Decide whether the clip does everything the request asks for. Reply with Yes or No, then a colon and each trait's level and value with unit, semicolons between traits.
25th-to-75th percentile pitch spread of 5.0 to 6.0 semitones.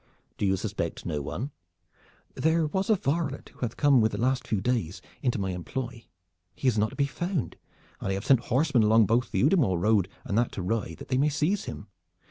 Yes: wide, 5.5 semitones